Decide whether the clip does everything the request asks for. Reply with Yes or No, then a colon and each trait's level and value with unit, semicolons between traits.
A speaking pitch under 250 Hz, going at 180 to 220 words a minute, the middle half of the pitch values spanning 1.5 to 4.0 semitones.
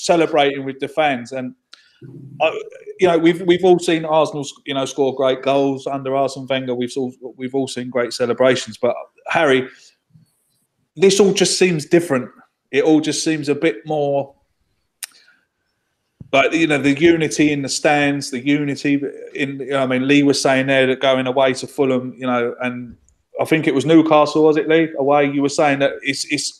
Yes: medium, 140 Hz; average, 190 wpm; average, 3.0 semitones